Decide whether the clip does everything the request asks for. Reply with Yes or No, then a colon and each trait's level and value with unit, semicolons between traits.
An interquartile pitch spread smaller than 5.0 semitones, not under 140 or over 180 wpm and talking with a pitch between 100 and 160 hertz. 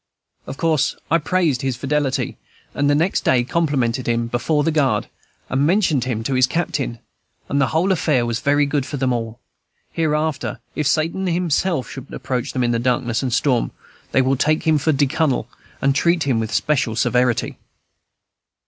Yes: average, 3.9 semitones; average, 175 wpm; medium, 140 Hz